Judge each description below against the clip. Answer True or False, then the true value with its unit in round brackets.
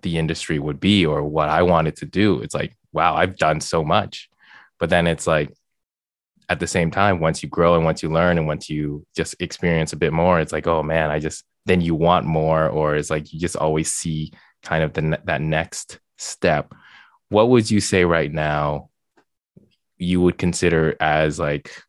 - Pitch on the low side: True (80 Hz)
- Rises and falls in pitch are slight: True (2.1 semitones)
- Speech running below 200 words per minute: False (205 wpm)